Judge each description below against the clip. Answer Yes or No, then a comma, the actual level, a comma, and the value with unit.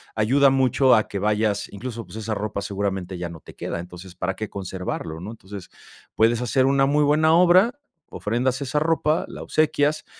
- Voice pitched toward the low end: Yes, low, 110 Hz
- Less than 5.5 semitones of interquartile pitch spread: No, wide, 5.9 semitones